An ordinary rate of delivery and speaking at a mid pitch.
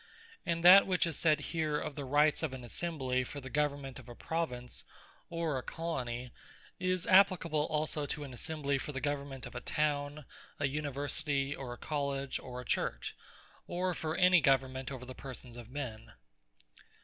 Yes: average, 180 wpm; medium, 145 Hz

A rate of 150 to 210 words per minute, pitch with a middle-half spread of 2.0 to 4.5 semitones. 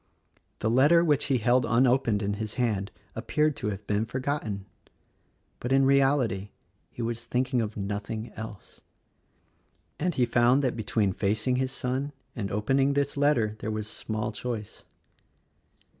Yes: average, 160 wpm; average, 4.0 semitones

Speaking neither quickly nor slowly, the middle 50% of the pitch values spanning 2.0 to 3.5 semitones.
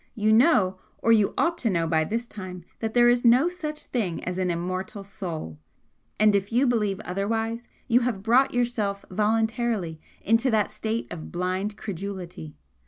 No: average, 170 wpm; average, 4.2 semitones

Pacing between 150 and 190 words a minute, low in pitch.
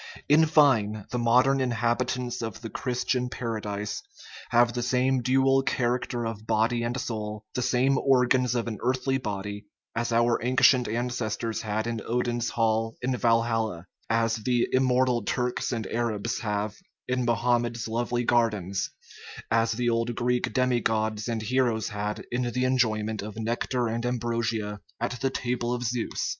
Yes: average, 155 wpm; low, 120 Hz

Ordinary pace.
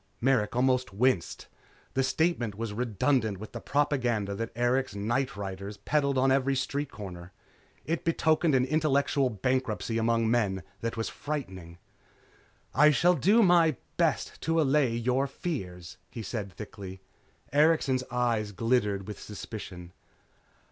No: slow, 130 wpm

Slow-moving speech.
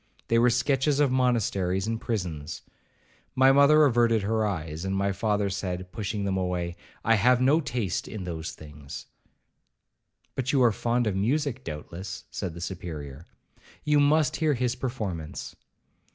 No: average, 150 wpm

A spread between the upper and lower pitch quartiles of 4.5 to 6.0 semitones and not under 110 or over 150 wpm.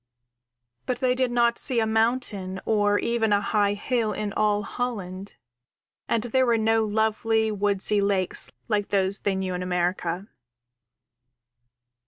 No: narrow, 2.5 semitones; average, 140 wpm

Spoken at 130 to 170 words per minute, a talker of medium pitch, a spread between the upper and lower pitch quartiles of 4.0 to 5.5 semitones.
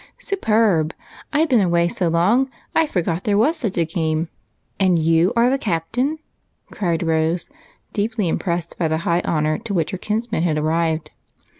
Yes: average, 160 wpm; medium, 175 Hz; average, 5.2 semitones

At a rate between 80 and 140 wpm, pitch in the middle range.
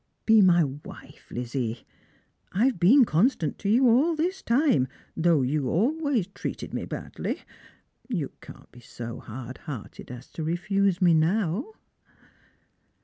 Yes: slow, 135 wpm; medium, 175 Hz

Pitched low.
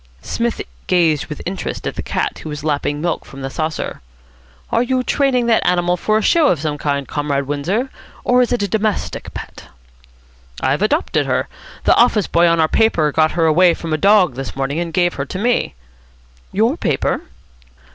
No: medium, 175 Hz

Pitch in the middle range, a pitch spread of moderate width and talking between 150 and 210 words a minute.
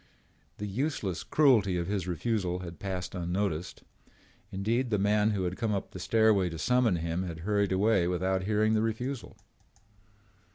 No: low, 100 Hz; average, 3.3 semitones; average, 160 wpm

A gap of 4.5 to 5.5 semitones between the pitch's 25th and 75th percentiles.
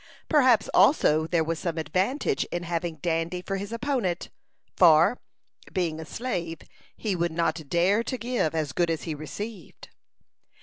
No: average, 4.1 semitones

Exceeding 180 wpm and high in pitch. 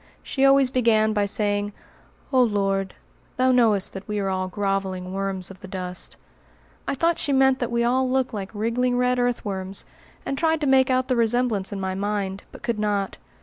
Yes: average, 190 wpm; high, 215 Hz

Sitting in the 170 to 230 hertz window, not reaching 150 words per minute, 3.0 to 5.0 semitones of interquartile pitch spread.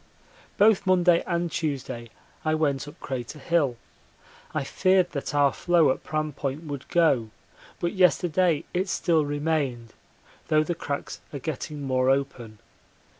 No: medium, 150 Hz; average, 140 wpm; average, 4.0 semitones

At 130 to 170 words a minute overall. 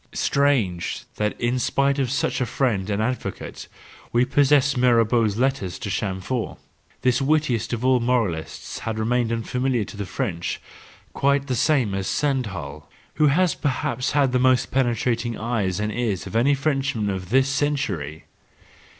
Yes: average, 150 wpm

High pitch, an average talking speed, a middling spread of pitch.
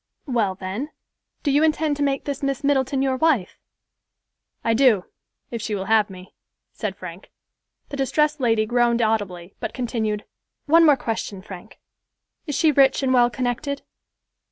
Yes: high, 245 Hz; average, 155 wpm; average, 4.8 semitones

